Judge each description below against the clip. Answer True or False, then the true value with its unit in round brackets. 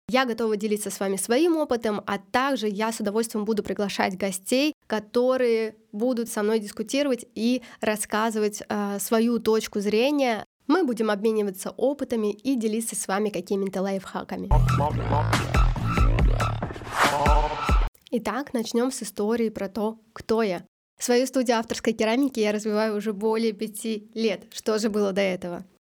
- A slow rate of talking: False (135 wpm)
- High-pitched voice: True (220 Hz)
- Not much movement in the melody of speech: True (2.3 semitones)